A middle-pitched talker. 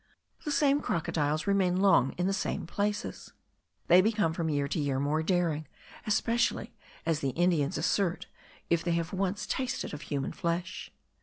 Yes: medium, 175 Hz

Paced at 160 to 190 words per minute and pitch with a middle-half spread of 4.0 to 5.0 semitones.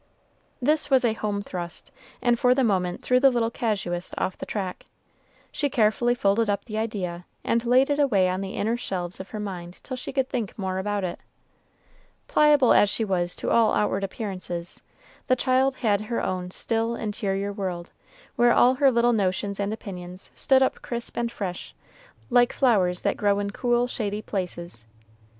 Yes: average, 180 wpm; average, 4.3 semitones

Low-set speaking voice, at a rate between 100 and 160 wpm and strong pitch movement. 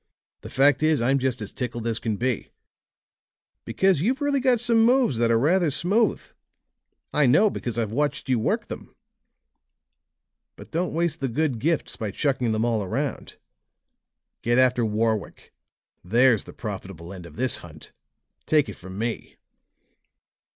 Yes: low, 125 Hz; average, 155 wpm; wide, 6.0 semitones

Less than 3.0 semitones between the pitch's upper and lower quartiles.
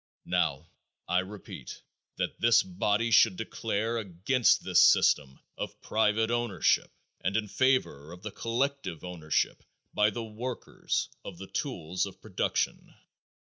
No: average, 4.2 semitones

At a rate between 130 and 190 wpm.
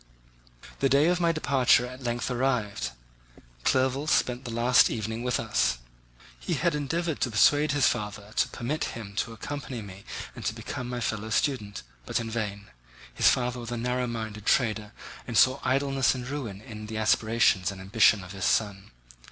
Yes: average, 175 wpm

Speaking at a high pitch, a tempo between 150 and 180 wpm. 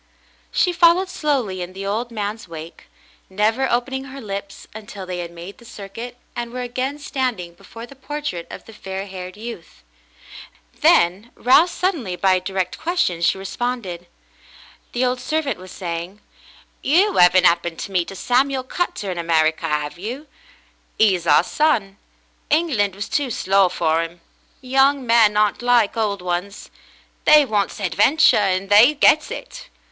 Yes: high, 210 Hz; average, 160 wpm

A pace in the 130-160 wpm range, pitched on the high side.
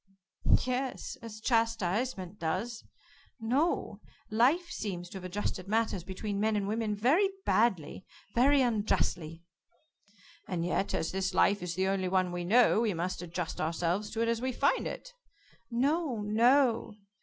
Yes: average, 145 wpm; high, 210 Hz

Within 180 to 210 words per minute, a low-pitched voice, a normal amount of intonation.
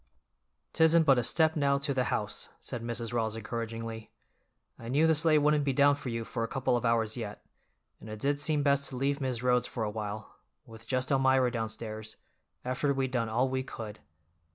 Yes: average, 200 wpm; low, 125 Hz; average, 3.5 semitones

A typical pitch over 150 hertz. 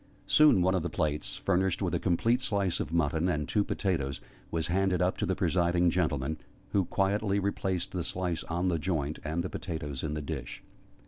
No: very low, 85 Hz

